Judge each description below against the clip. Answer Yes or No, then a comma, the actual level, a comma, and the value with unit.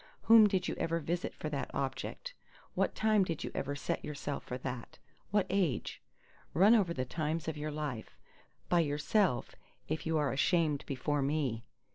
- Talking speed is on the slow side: No, average, 165 wpm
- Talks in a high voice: No, medium, 155 Hz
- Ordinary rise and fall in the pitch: Yes, average, 4.1 semitones